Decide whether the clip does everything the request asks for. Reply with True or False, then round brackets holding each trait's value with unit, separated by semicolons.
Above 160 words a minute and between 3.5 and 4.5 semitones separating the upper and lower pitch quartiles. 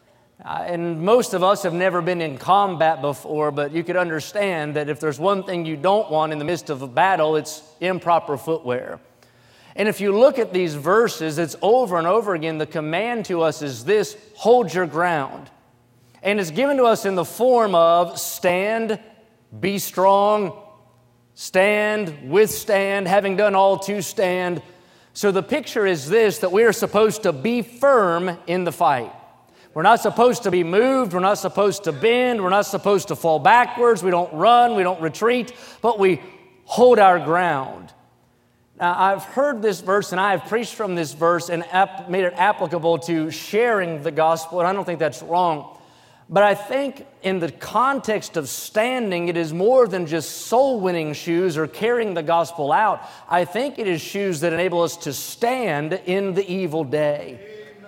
True (180 wpm; 4.1 semitones)